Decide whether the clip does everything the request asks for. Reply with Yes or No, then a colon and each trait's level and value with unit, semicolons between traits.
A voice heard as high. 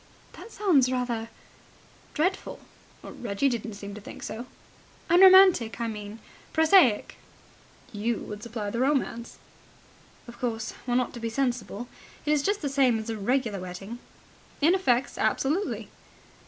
Yes: high, 240 Hz